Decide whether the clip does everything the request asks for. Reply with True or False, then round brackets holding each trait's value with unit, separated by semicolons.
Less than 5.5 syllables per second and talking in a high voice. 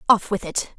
True (4.9 syllables/s; 200 Hz)